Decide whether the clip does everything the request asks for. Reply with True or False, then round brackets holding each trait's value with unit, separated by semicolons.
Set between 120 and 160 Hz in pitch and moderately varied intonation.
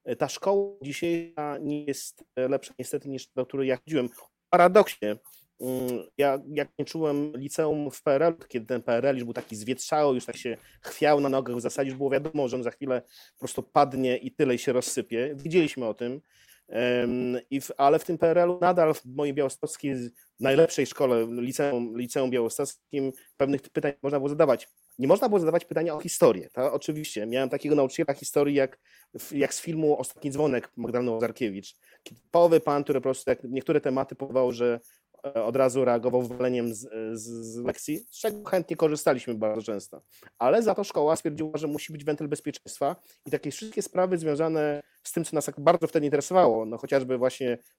True (140 Hz; 3.7 semitones)